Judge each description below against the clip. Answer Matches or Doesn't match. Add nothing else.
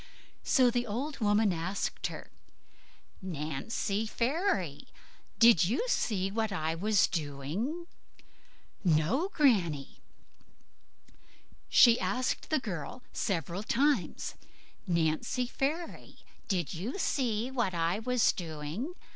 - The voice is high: Matches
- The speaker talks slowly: Matches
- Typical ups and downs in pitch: Doesn't match